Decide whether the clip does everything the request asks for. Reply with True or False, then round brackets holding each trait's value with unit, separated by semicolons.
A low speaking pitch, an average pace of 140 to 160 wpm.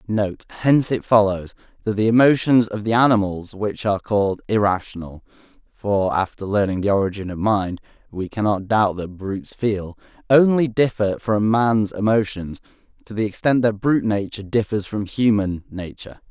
True (105 Hz; 150 wpm)